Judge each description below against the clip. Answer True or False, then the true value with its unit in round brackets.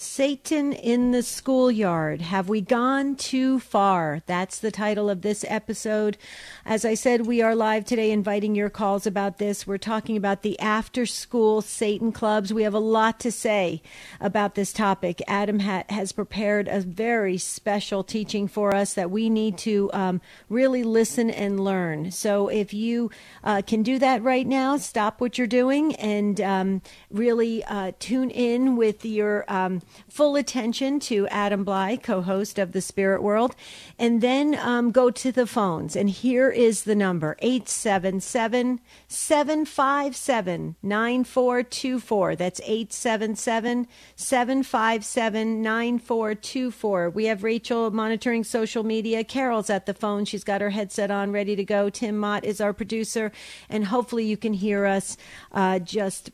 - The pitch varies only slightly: False (3.1 semitones)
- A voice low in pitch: False (215 Hz)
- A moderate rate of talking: True (155 wpm)